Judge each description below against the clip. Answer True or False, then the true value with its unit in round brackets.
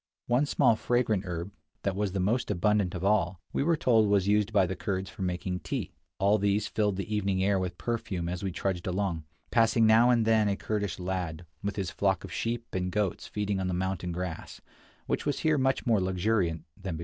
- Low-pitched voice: True (100 Hz)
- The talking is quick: True (215 wpm)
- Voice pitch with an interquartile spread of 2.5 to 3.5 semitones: True (3.0 semitones)